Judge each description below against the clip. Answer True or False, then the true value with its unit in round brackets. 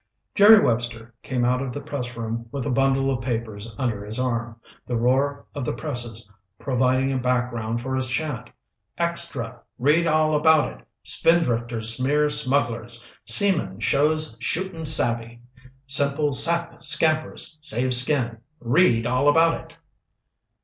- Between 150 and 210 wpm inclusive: False (135 wpm)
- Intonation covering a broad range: False (4.2 semitones)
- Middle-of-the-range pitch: False (130 Hz)